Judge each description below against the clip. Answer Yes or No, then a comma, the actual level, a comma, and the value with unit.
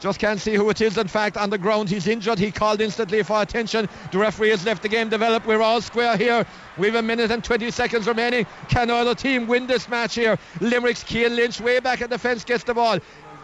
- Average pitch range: No, narrow, 1.9 semitones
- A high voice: Yes, high, 225 Hz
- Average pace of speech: No, fast, 245 wpm